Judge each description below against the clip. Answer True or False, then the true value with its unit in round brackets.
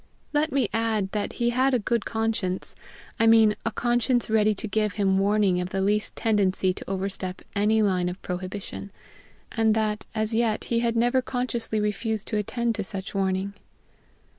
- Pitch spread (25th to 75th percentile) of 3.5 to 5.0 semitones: False (2.8 semitones)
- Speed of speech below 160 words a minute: False (175 wpm)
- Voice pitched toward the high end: True (215 Hz)